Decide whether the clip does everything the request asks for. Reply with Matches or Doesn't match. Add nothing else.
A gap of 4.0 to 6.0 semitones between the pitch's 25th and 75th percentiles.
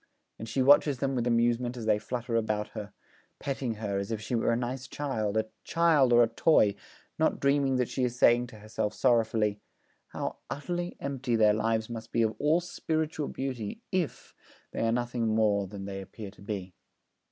Doesn't match